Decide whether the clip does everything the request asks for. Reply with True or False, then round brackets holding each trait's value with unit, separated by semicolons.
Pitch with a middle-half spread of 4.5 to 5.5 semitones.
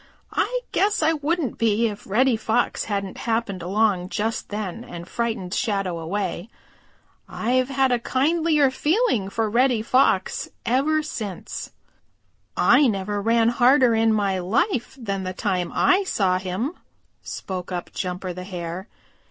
True (5.2 semitones)